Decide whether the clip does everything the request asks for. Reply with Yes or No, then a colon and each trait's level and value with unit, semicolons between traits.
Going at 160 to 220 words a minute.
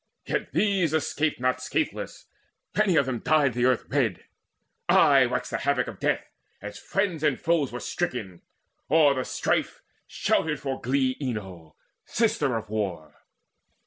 No: average, 145 wpm